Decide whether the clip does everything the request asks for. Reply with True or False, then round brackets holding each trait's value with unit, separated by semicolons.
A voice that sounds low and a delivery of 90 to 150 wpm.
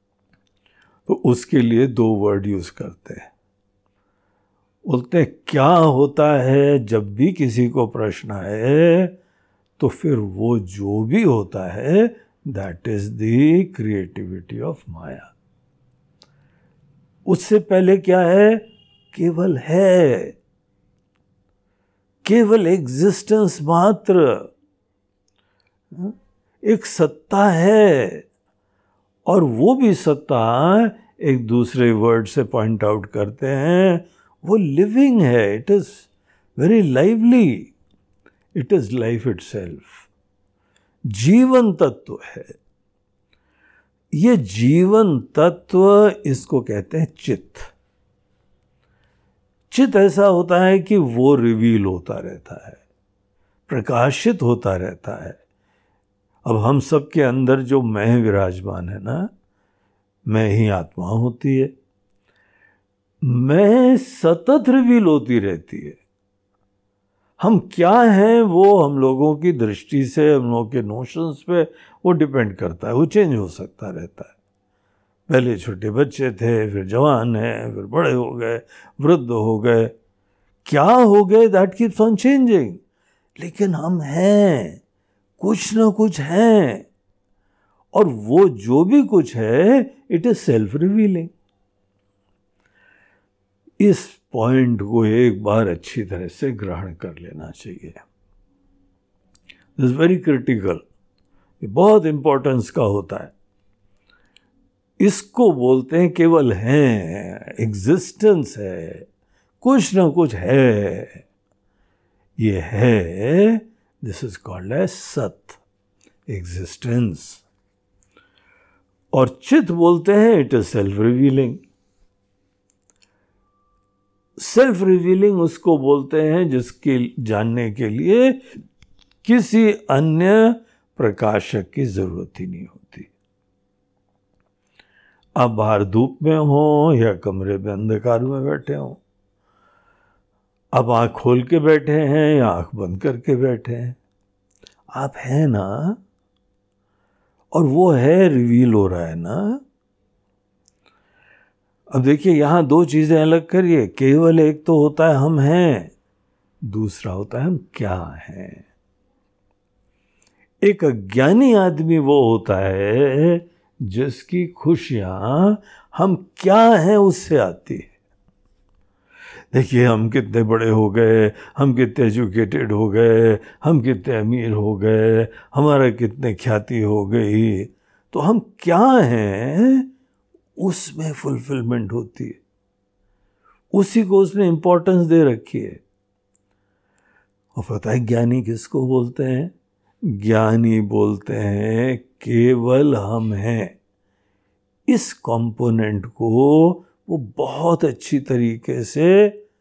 True (125 Hz; 110 wpm)